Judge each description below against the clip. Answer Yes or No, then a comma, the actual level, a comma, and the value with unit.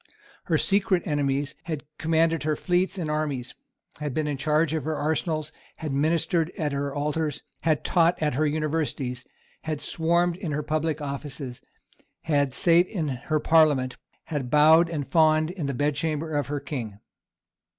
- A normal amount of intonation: No, narrow, 2.2 semitones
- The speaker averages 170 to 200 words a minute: No, average, 160 wpm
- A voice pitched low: No, medium, 155 Hz